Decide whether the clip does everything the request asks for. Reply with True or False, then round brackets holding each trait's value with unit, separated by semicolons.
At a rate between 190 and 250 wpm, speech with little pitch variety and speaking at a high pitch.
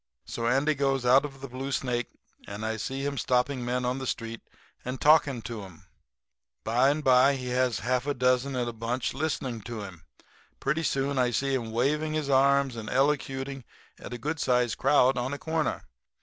False (200 wpm; 2.3 semitones; 130 Hz)